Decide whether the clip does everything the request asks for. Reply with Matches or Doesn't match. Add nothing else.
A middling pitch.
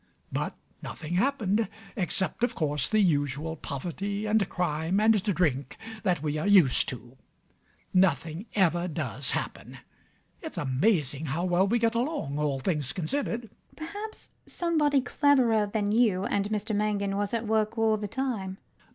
Doesn't match